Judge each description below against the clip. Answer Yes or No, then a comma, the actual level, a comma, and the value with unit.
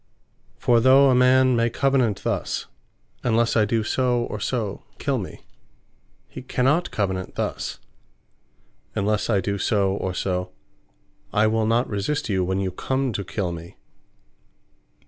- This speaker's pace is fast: No, average, 145 wpm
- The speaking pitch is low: Yes, low, 110 Hz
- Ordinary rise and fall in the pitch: Yes, average, 4.4 semitones